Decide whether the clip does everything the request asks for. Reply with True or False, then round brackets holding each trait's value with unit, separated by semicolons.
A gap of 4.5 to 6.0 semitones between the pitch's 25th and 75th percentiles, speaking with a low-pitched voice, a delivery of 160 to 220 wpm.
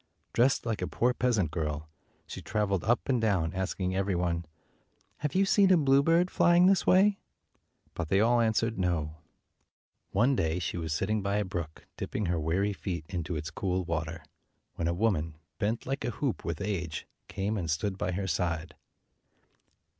True (5.6 semitones; 95 Hz; 175 wpm)